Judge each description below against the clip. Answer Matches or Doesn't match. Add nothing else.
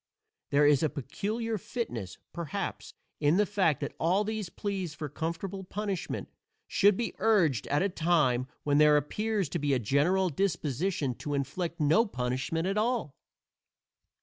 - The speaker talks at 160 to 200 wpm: Doesn't match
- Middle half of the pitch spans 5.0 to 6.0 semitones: Matches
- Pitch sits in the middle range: Matches